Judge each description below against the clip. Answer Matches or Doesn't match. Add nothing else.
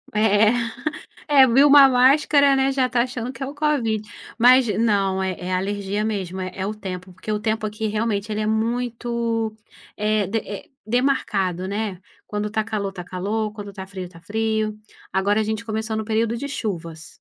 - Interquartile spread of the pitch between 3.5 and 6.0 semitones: Doesn't match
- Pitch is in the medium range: Doesn't match